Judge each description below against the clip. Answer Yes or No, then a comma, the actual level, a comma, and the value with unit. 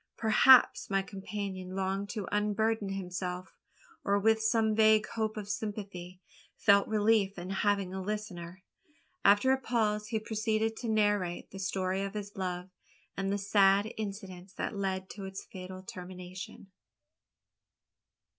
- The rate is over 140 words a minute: No, slow, 135 wpm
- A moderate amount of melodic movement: No, narrow, 2.3 semitones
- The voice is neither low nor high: No, high, 200 Hz